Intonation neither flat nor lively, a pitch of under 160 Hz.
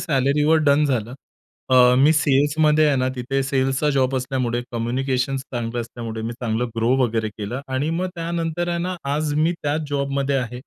Yes: average, 3.3 semitones; low, 135 Hz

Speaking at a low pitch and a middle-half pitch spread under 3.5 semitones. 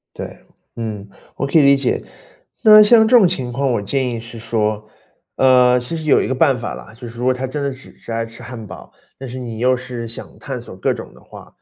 Yes: low, 125 Hz; average, 3.1 semitones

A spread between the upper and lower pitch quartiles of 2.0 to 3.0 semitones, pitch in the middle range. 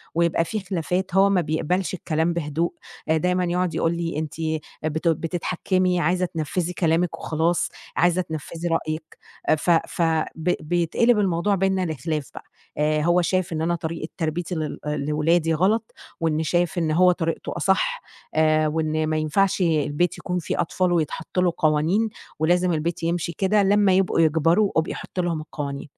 Yes: narrow, 2.4 semitones; medium, 170 Hz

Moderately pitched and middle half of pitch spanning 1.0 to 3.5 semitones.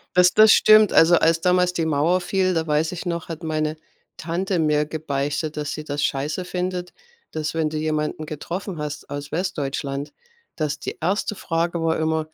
Yes: medium, 160 Hz; average, 2.9 semitones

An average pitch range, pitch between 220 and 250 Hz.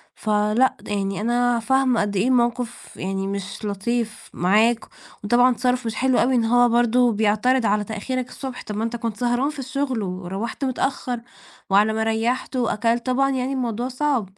Yes: average, 3.1 semitones; high, 235 Hz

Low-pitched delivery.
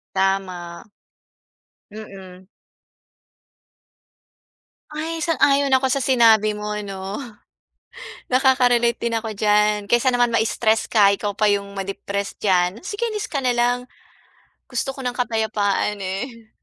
No: high, 220 Hz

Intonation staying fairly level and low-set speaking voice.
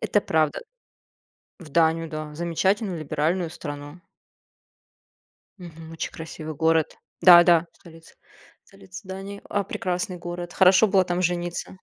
No: narrow, 2.3 semitones; medium, 170 Hz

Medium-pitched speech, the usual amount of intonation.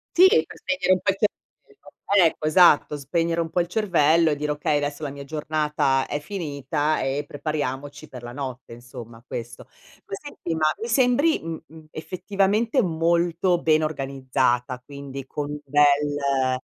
Yes: medium, 150 Hz; average, 3.7 semitones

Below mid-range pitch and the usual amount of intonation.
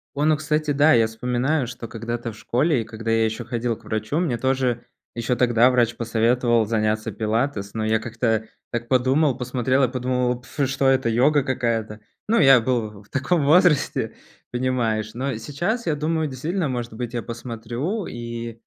Yes: low, 120 Hz; average, 3.1 semitones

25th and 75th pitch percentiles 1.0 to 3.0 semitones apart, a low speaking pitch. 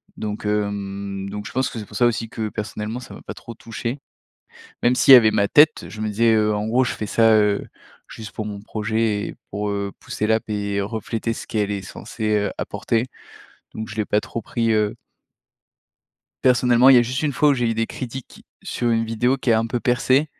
Yes: narrow, 2.4 semitones; low, 110 Hz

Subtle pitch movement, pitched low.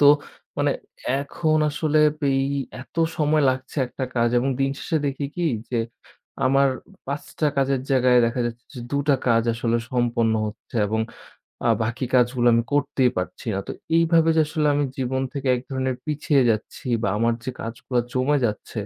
No: average, 3.3 semitones; low, 130 Hz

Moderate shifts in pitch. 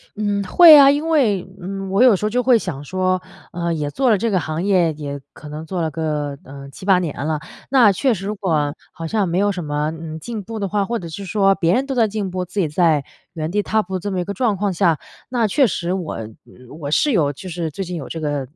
Yes: average, 4.6 semitones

